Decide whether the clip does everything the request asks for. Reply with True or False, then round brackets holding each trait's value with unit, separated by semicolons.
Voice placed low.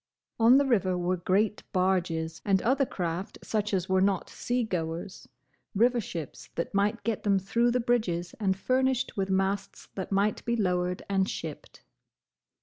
False (195 Hz)